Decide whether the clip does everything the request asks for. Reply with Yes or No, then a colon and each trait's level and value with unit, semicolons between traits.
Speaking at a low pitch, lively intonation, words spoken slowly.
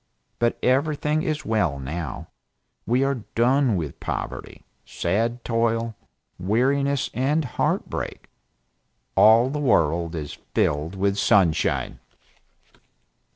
Yes: low, 115 Hz; wide, 7.4 semitones; slow, 105 wpm